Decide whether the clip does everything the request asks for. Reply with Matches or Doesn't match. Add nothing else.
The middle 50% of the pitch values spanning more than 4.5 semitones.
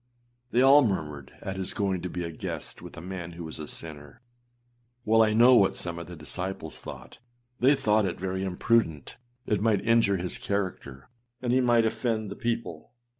Matches